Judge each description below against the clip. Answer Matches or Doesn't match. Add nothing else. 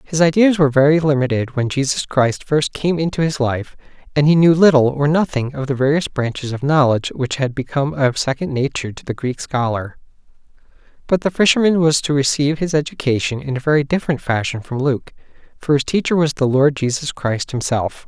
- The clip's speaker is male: Matches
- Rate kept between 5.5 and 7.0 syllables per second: Matches